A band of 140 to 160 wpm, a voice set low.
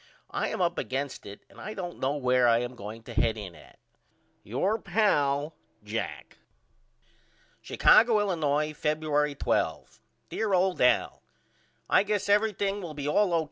No: average, 150 wpm; medium, 150 Hz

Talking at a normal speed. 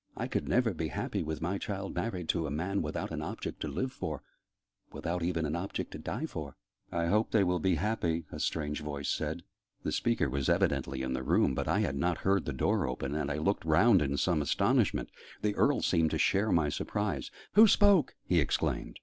No: fast, 215 wpm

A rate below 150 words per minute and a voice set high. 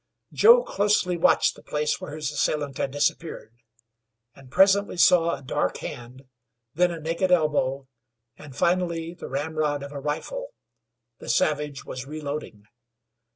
No: average, 140 wpm; medium, 150 Hz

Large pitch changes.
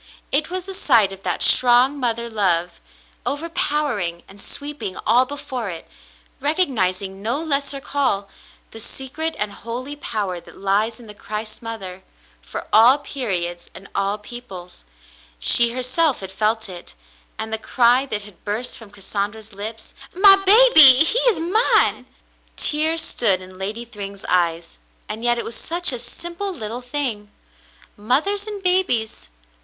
Yes: wide, 6.2 semitones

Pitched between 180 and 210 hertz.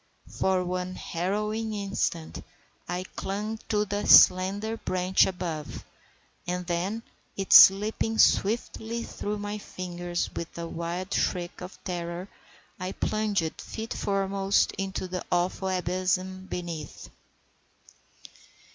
Yes: medium, 185 Hz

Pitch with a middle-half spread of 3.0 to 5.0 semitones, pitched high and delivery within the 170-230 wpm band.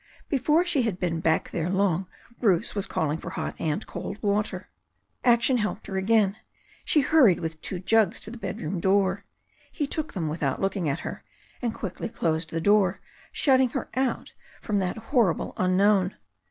Yes: average, 4.5 semitones; high, 200 Hz; average, 175 wpm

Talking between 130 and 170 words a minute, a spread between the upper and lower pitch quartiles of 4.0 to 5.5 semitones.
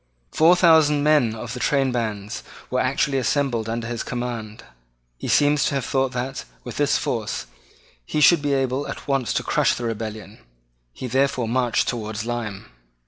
No: average, 165 wpm; average, 3.5 semitones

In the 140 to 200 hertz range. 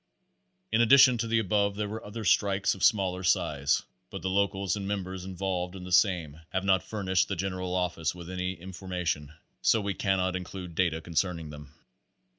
No: very low, 95 Hz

